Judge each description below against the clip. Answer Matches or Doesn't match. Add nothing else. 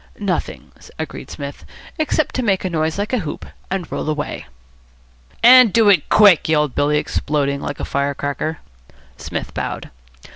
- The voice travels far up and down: Matches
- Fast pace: Doesn't match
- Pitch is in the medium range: Matches